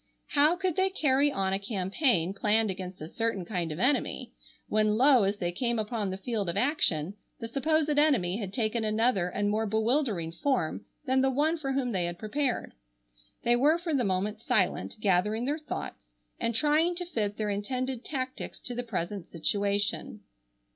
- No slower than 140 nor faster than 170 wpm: No, average, 180 wpm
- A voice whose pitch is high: Yes, high, 225 Hz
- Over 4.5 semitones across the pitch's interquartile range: Yes, wide, 5.6 semitones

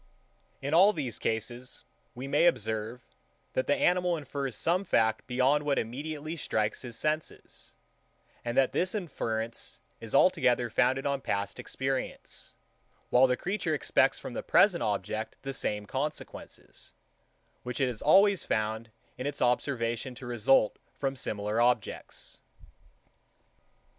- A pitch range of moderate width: Yes, average, 4.6 semitones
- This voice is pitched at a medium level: No, low, 130 Hz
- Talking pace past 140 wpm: No, slow, 135 wpm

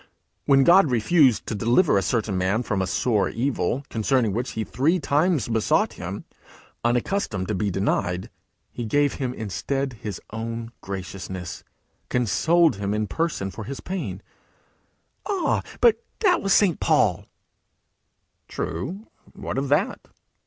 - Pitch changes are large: Yes, wide, 6.2 semitones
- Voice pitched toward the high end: No, low, 120 Hz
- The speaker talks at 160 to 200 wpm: No, average, 140 wpm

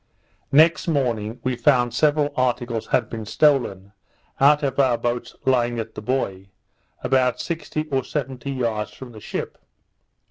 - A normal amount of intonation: Yes, average, 3.2 semitones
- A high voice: No, low, 125 Hz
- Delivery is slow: No, average, 145 wpm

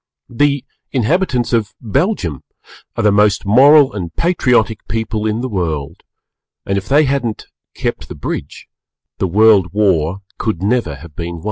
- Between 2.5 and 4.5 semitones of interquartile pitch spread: No, average, 5.2 semitones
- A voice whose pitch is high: No, low, 110 Hz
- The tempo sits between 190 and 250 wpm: No, average, 150 wpm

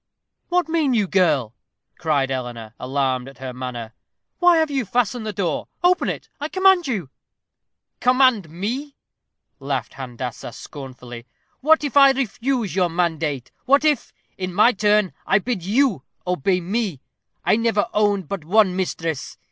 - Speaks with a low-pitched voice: No, high, 195 Hz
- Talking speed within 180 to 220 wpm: No, average, 150 wpm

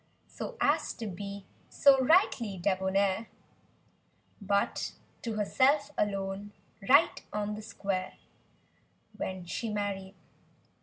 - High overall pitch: Yes, high, 205 Hz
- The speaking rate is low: Yes, slow, 100 wpm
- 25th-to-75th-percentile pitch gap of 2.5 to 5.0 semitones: Yes, average, 3.0 semitones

